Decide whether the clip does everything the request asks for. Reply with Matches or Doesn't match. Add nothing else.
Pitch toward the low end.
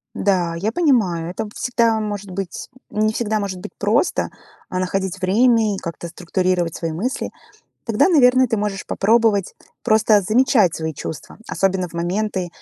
Doesn't match